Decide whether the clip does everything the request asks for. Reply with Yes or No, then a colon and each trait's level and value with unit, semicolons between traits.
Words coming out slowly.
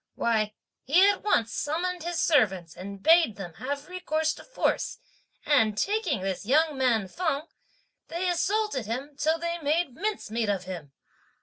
No: average, 150 wpm